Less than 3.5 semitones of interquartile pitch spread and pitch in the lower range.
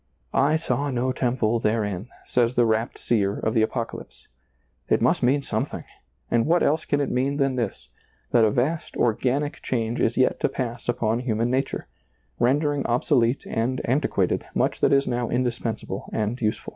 Yes: average, 2.9 semitones; low, 120 Hz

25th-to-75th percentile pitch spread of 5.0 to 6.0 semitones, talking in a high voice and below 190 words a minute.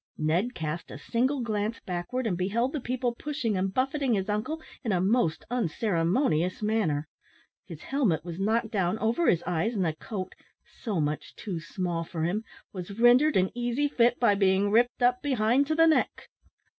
Yes: wide, 5.6 semitones; high, 215 Hz; average, 180 wpm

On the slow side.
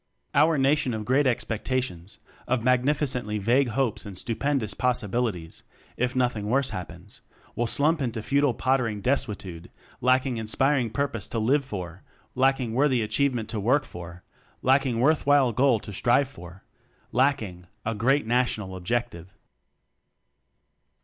Yes: slow, 130 wpm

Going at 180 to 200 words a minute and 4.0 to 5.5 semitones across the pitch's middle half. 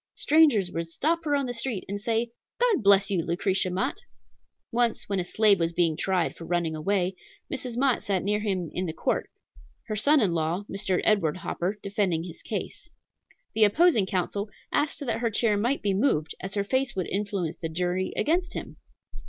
Yes: average, 190 wpm; average, 4.8 semitones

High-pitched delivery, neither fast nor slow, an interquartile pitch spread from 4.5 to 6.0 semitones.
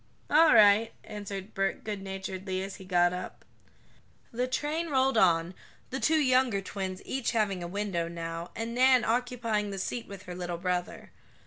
Yes: high, 200 Hz; average, 160 wpm; average, 4.9 semitones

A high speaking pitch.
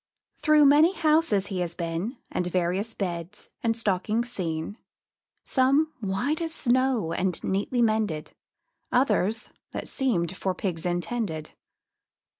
Yes: high, 210 Hz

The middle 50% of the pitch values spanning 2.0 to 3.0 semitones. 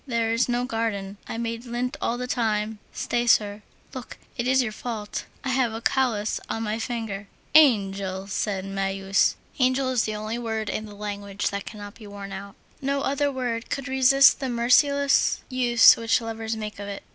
No: average, 3.4 semitones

